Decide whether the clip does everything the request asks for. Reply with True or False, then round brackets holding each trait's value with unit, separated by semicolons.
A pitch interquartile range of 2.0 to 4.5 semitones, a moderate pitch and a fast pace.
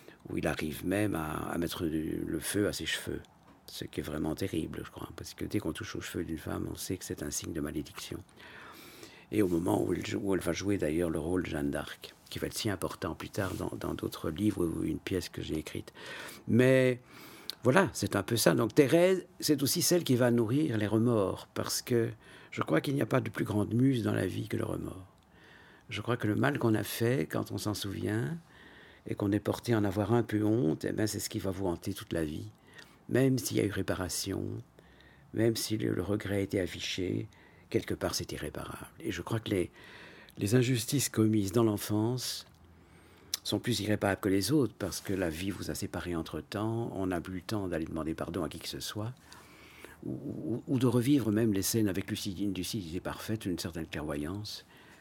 False (4.1 semitones; 105 Hz; 225 wpm)